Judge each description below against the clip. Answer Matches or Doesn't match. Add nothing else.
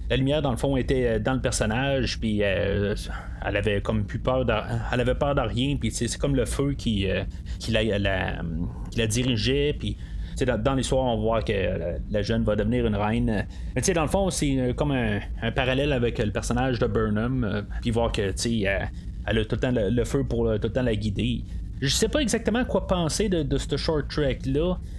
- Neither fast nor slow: Doesn't match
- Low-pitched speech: Matches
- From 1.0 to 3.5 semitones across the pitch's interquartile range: Doesn't match